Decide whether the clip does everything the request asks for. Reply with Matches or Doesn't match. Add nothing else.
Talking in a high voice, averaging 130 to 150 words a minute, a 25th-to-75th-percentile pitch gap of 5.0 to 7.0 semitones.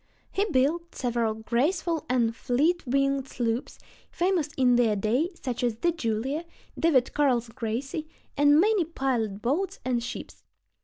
Matches